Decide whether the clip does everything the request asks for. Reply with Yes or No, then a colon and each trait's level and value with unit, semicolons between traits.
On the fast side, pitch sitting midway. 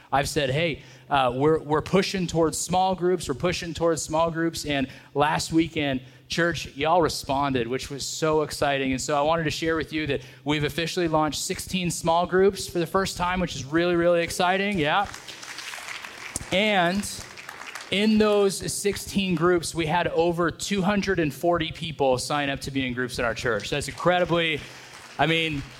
No: average, 170 wpm; medium, 165 Hz